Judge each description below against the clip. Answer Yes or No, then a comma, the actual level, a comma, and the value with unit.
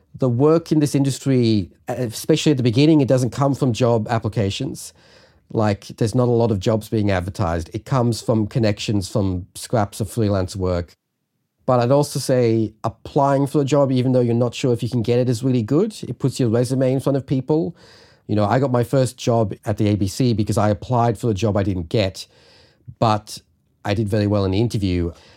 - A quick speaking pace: Yes, fast, 210 wpm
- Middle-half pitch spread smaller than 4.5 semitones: Yes, average, 3.7 semitones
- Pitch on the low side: Yes, low, 120 Hz